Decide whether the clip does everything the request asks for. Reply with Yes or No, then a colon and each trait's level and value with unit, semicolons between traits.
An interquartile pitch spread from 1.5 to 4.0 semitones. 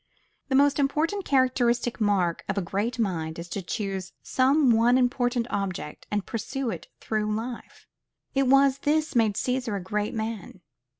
No: average, 4.5 semitones